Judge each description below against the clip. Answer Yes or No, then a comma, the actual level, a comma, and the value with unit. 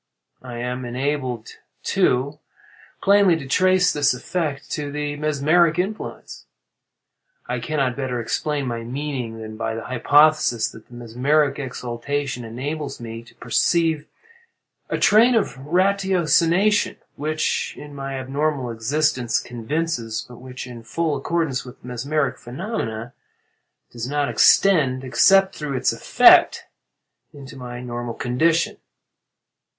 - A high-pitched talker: No, medium, 140 Hz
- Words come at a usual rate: No, slow, 125 wpm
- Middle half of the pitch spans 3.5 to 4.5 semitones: Yes, average, 4.2 semitones